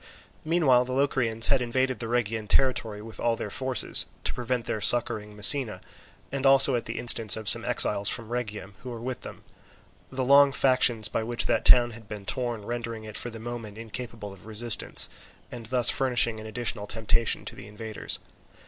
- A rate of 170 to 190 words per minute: Yes, average, 185 wpm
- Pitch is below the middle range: Yes, low, 115 Hz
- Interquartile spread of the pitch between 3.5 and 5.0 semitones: No, narrow, 2.6 semitones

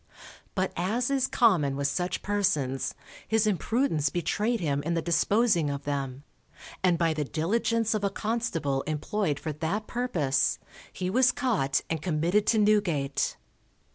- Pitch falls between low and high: Yes, medium, 175 Hz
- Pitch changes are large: Yes, wide, 6.5 semitones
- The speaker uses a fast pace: No, average, 145 wpm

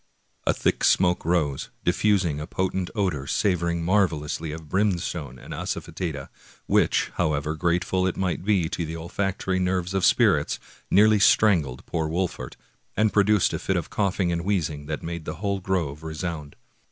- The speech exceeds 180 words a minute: No, average, 165 wpm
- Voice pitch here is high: No, very low, 85 Hz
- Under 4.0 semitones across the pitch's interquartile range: Yes, average, 3.4 semitones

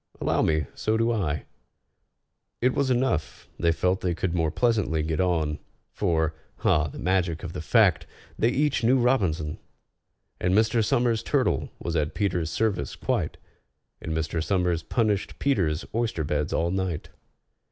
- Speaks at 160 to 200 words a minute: No, average, 150 wpm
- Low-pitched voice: Yes, very low, 90 Hz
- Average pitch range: No, wide, 5.8 semitones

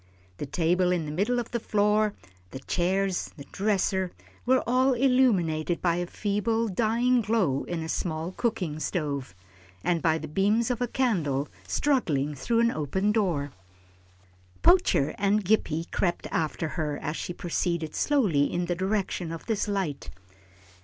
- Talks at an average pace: Yes, average, 155 wpm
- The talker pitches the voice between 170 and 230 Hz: Yes, medium, 185 Hz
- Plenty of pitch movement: Yes, wide, 5.7 semitones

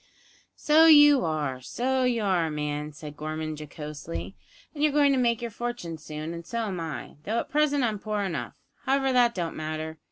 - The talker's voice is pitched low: No, high, 190 Hz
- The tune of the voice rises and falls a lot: Yes, wide, 8.4 semitones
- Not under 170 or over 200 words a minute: Yes, average, 190 wpm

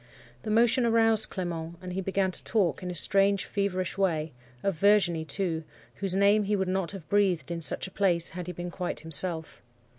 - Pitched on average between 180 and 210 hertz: Yes, medium, 185 Hz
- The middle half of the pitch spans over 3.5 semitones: No, average, 2.8 semitones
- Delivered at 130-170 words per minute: No, average, 190 wpm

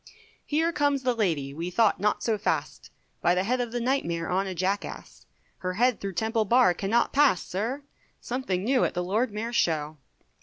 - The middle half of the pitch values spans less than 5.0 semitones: No, average, 5.3 semitones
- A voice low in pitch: No, high, 210 Hz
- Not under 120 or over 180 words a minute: No, average, 195 wpm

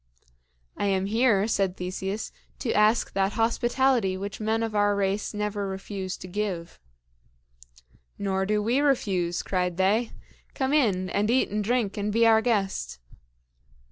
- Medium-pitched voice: No, high, 205 Hz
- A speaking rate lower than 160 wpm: Yes, average, 145 wpm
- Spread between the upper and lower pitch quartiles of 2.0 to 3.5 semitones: Yes, average, 2.8 semitones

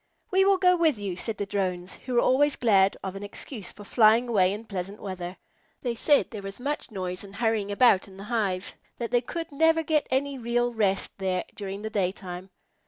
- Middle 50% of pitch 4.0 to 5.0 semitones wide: Yes, average, 4.5 semitones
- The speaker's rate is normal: No, fast, 215 wpm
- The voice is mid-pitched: No, high, 210 Hz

